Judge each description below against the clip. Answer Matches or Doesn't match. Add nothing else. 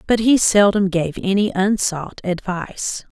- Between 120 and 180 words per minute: Matches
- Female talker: Matches